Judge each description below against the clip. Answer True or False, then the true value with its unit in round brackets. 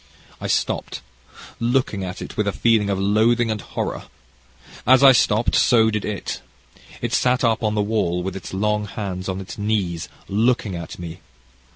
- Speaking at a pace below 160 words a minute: False (175 wpm)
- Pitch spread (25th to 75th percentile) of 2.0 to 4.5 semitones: True (2.9 semitones)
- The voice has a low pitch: True (105 Hz)